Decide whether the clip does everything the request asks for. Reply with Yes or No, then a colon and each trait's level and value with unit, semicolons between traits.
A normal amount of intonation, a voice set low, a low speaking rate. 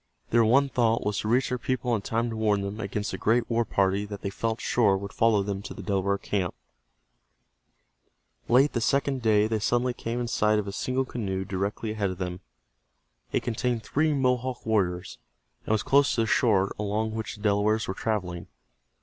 No: average, 3.2 semitones; low, 110 Hz; average, 200 wpm